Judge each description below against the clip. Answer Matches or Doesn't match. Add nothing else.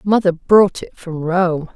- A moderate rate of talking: Matches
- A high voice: Doesn't match